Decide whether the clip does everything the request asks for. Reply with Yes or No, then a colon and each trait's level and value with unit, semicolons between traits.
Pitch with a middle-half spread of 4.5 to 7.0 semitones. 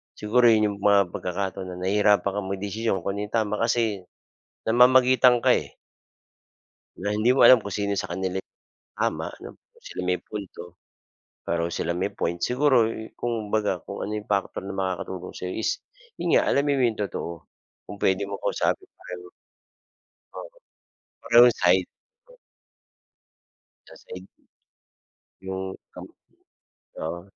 No: average, 3.2 semitones